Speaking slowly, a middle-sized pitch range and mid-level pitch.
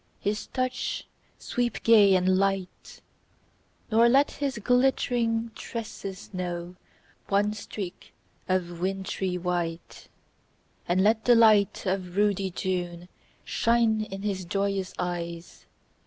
No: slow, 110 wpm; average, 3.6 semitones; high, 195 Hz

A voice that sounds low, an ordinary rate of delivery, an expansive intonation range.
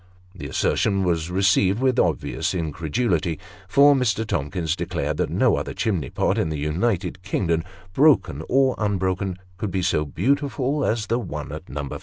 Yes: very low, 95 Hz; average, 165 wpm; wide, 6.2 semitones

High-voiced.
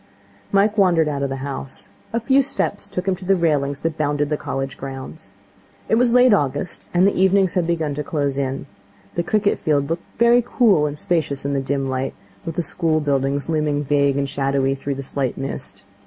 No: medium, 150 Hz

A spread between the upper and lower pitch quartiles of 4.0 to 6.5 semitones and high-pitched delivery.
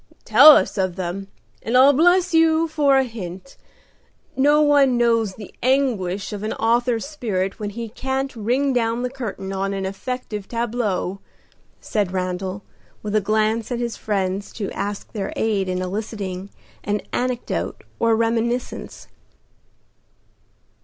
Yes: average, 4.3 semitones; high, 225 Hz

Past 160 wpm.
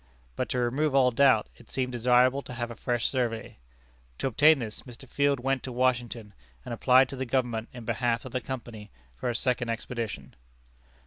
Yes: average, 190 wpm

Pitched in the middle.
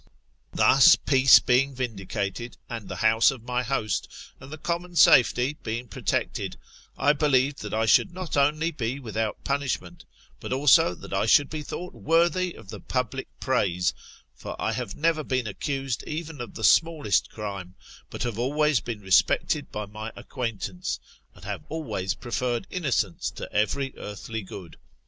No: low, 125 Hz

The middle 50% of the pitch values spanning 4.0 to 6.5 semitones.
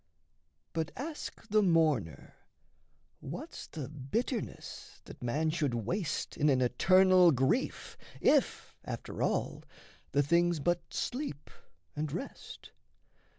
Yes: average, 4.8 semitones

